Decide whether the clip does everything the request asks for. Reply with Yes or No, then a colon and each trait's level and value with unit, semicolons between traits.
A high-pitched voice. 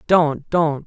No: medium, 155 Hz